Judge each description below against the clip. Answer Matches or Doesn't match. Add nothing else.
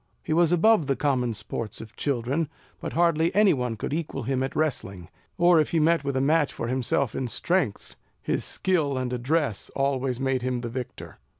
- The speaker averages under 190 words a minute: Doesn't match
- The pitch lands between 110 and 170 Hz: Matches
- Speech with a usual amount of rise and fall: Matches